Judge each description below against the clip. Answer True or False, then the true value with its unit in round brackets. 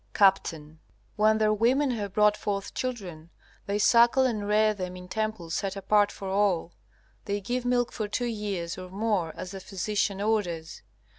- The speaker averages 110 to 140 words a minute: False (165 wpm)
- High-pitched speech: True (205 Hz)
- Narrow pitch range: True (2.3 semitones)